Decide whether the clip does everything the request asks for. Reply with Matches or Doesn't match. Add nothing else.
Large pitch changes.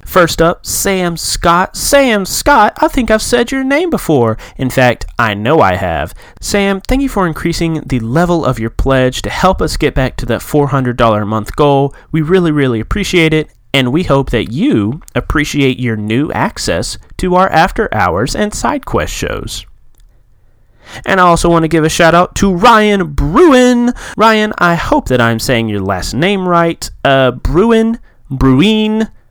Matches